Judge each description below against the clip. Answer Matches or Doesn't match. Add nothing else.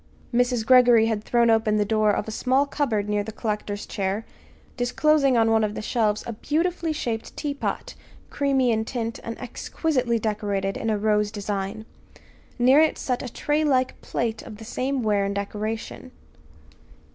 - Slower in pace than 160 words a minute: Doesn't match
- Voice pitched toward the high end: Matches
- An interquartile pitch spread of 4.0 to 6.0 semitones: Doesn't match